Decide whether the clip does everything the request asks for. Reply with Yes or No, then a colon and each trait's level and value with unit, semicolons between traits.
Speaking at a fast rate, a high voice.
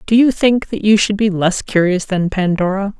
Yes: fast, 220 wpm; high, 200 Hz